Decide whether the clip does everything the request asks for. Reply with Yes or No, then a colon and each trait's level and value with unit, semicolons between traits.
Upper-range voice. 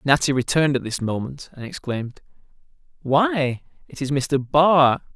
No: low, 135 Hz